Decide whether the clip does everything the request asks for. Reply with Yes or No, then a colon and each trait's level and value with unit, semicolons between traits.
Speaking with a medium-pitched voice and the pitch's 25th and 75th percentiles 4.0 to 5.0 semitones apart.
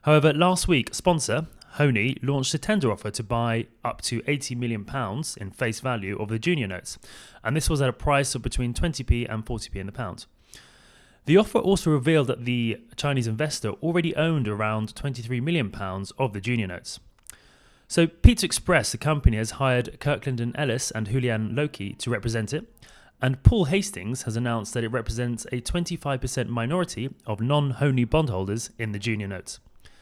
No: low, 125 Hz; average, 4.7 semitones